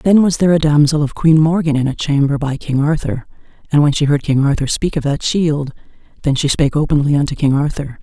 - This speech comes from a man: No, female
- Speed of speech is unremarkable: No, fast, 230 wpm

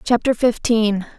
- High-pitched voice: Yes, high, 225 Hz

